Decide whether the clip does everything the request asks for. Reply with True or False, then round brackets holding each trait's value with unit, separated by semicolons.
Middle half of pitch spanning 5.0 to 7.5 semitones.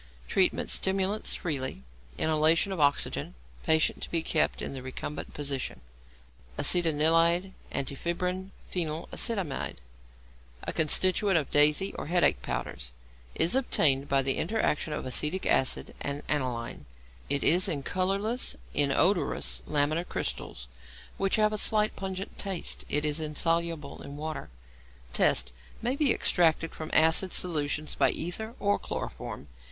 False (4.5 semitones)